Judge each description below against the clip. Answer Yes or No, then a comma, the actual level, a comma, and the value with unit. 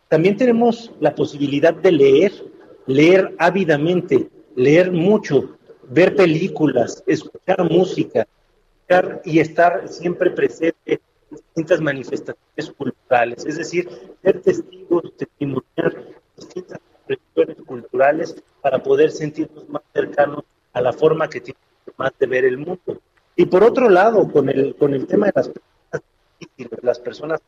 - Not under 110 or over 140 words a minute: Yes, average, 130 wpm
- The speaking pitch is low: No, medium, 175 Hz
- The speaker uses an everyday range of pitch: No, wide, 7.5 semitones